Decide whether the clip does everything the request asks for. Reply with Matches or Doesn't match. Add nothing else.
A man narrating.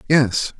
Matches